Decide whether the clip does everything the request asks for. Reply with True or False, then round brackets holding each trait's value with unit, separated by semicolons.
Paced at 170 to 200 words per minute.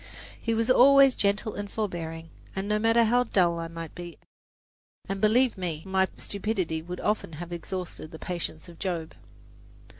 False (155 wpm)